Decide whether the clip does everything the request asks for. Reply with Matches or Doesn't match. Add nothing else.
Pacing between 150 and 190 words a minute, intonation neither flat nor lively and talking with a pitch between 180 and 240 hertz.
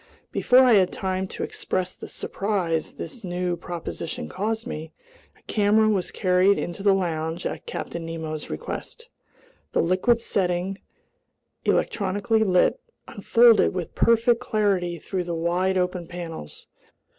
Doesn't match